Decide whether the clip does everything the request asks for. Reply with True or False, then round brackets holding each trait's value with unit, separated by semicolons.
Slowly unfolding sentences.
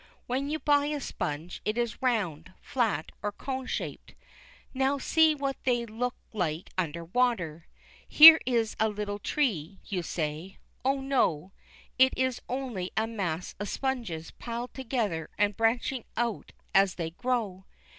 False (145 wpm)